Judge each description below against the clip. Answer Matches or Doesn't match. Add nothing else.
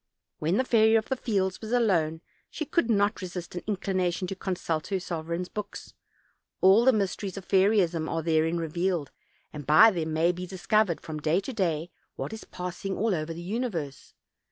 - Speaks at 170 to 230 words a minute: Matches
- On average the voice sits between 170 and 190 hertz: Matches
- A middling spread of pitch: Matches